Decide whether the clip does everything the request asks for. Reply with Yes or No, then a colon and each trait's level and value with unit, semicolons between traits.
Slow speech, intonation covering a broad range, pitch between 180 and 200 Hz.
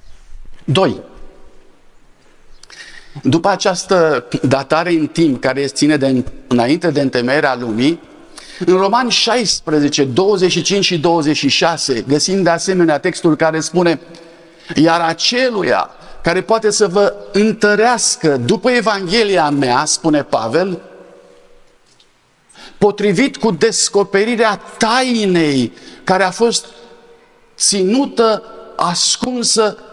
Yes: slow, 95 wpm; wide, 6.5 semitones; medium, 185 Hz